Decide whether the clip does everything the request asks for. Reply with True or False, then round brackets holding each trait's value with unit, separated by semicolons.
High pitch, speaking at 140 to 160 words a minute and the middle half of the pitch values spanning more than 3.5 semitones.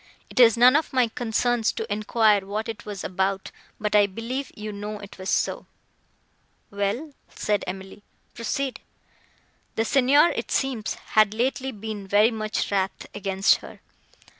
False (215 Hz; 145 wpm; 3.2 semitones)